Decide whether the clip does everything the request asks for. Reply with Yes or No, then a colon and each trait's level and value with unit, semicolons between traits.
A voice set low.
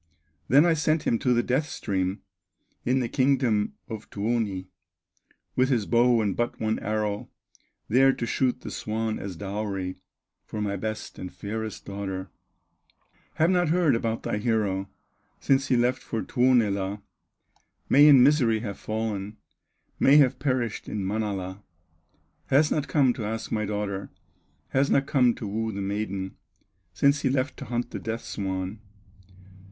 Yes: low, 110 Hz